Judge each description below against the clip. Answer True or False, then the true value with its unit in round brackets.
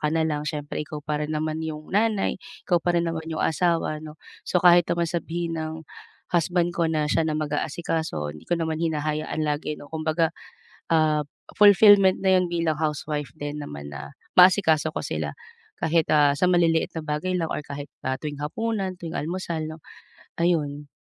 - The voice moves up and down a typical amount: False (2.3 semitones)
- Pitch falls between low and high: True (160 Hz)